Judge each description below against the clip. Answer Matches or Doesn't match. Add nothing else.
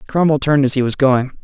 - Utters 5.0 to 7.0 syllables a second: Matches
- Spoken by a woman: Doesn't match